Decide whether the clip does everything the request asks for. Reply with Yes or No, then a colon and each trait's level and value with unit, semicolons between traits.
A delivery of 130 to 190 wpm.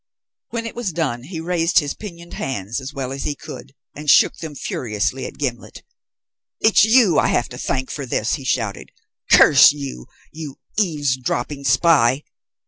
Yes: average, 165 wpm